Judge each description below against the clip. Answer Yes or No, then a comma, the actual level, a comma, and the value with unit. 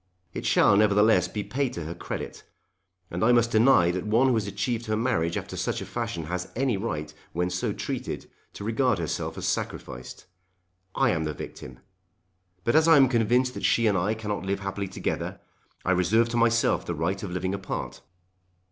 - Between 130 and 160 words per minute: No, average, 190 wpm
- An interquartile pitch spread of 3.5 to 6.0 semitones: Yes, average, 4.7 semitones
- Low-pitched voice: Yes, low, 100 Hz